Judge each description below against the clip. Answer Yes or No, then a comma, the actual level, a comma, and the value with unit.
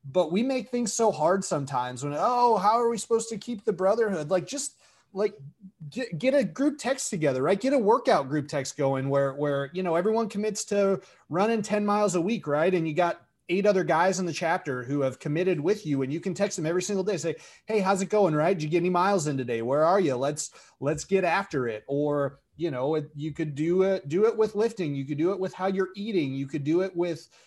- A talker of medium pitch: Yes, medium, 180 Hz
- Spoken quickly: Yes, fast, 250 wpm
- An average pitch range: No, wide, 5.7 semitones